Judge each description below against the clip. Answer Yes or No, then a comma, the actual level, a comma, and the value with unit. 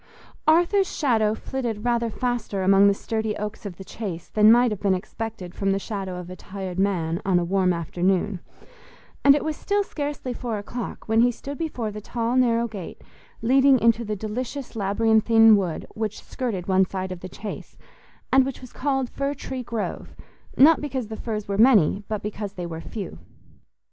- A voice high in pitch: Yes, high, 220 Hz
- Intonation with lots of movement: No, average, 4.2 semitones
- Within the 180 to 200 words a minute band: Yes, average, 185 wpm